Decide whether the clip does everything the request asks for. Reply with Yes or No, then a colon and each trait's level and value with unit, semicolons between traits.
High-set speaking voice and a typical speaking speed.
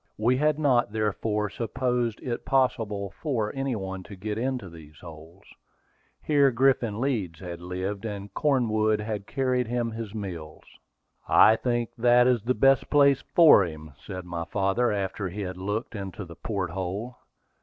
No: low, 110 Hz; average, 160 wpm